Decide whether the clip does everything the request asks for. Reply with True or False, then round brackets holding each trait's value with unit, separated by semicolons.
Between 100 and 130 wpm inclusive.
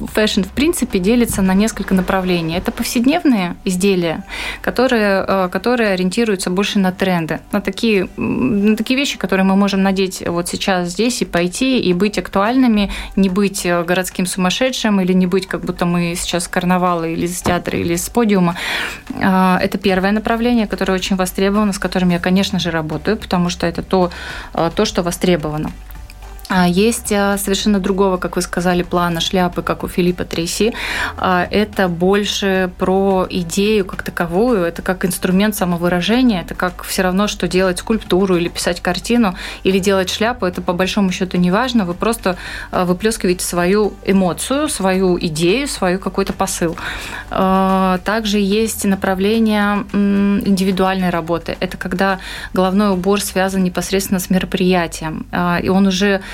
False (145 wpm)